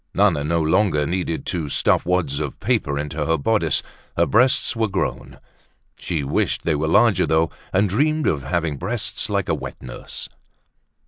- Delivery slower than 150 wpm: No, average, 170 wpm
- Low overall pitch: Yes, very low, 85 Hz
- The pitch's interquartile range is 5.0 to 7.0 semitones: Yes, wide, 5.5 semitones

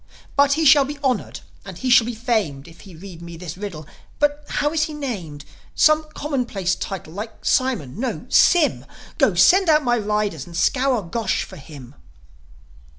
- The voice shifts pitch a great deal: Yes, wide, 8.4 semitones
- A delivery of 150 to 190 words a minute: Yes, average, 175 wpm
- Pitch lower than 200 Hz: No, high, 220 Hz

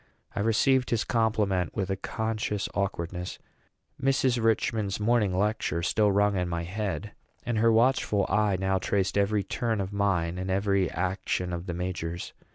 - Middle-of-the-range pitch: No, low, 100 Hz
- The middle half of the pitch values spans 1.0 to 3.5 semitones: Yes, average, 3.1 semitones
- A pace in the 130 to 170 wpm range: Yes, average, 160 wpm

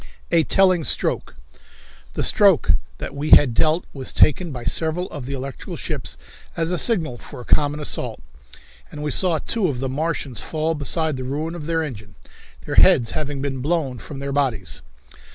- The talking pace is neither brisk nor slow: Yes, average, 180 wpm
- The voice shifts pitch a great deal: No, average, 3.5 semitones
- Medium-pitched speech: Yes, medium, 150 Hz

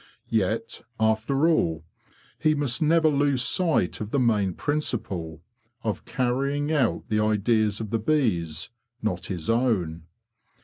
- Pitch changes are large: Yes, wide, 6.3 semitones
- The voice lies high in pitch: No, low, 115 Hz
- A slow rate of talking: Yes, slow, 130 wpm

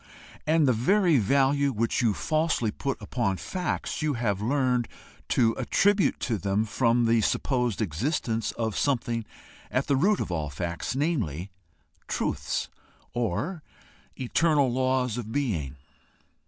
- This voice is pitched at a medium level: No, low, 125 Hz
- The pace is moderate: No, slow, 130 wpm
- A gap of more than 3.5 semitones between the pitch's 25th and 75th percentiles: Yes, average, 4.5 semitones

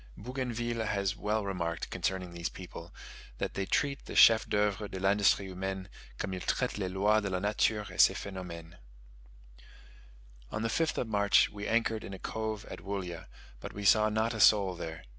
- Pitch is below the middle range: Yes, low, 100 Hz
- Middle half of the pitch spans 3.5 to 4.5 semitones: No, average, 2.7 semitones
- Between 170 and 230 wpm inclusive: Yes, average, 180 wpm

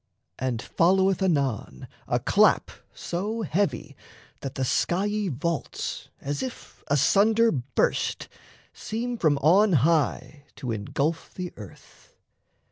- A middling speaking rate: No, slow, 110 wpm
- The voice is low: No, medium, 165 Hz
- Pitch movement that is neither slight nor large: No, wide, 6.2 semitones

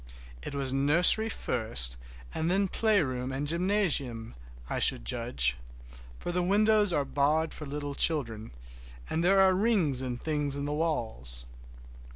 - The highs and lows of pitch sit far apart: Yes, wide, 6.2 semitones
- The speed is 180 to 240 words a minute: No, average, 145 wpm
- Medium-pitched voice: Yes, medium, 145 Hz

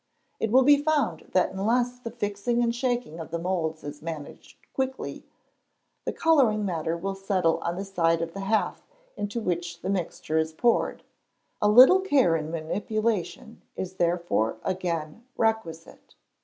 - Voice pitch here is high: Yes, high, 195 Hz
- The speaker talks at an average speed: Yes, average, 155 wpm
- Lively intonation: Yes, wide, 5.8 semitones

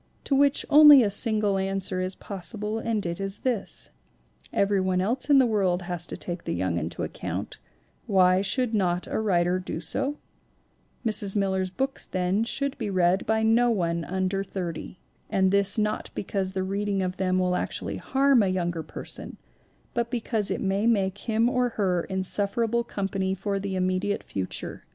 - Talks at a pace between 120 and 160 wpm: No, average, 170 wpm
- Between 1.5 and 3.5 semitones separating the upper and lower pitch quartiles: Yes, average, 3.2 semitones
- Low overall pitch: No, high, 195 Hz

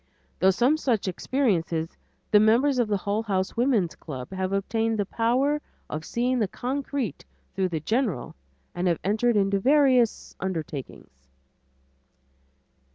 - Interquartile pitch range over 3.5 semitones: Yes, average, 5.1 semitones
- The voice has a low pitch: No, high, 210 Hz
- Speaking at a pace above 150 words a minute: No, slow, 135 wpm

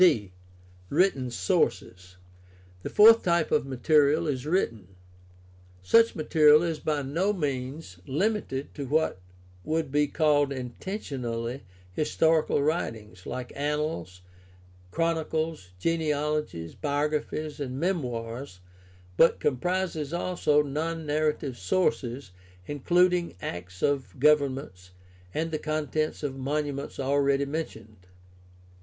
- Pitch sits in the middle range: Yes, medium, 145 Hz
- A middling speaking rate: No, slow, 110 wpm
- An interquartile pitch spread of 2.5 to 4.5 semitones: Yes, average, 4.1 semitones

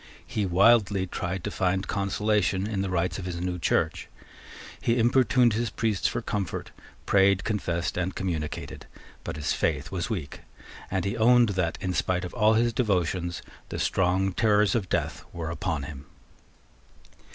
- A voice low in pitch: Yes, very low, 95 Hz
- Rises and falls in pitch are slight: No, average, 3.4 semitones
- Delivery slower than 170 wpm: Yes, average, 160 wpm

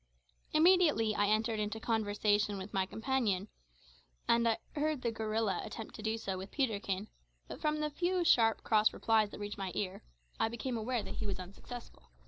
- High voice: Yes, high, 220 Hz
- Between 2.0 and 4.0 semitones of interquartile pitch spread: Yes, average, 2.9 semitones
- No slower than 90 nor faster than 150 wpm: No, average, 180 wpm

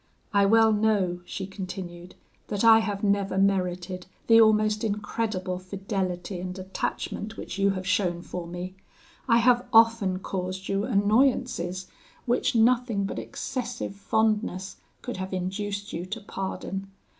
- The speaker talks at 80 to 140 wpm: Yes, slow, 135 wpm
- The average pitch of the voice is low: No, high, 200 Hz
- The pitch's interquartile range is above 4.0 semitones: No, average, 3.0 semitones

